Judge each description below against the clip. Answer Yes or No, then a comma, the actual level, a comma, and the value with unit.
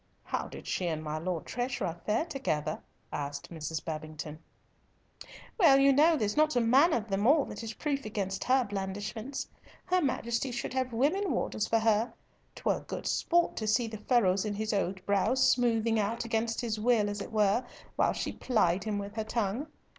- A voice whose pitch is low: No, high, 220 Hz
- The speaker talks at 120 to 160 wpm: No, average, 185 wpm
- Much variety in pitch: No, average, 4.3 semitones